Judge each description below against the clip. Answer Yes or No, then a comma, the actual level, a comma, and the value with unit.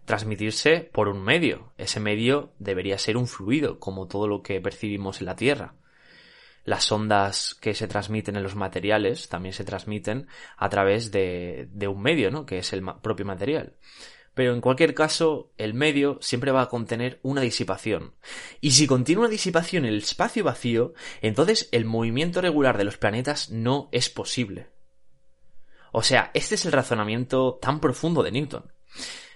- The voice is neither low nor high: No, low, 115 Hz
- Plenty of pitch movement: Yes, wide, 5.7 semitones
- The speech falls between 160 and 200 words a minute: Yes, average, 170 wpm